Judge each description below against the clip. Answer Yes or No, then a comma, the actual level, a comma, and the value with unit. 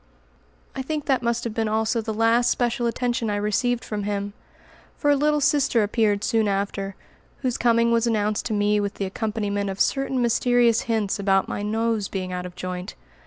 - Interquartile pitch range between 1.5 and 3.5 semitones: Yes, average, 2.8 semitones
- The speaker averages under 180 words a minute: No, average, 190 wpm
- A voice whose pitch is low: No, high, 220 Hz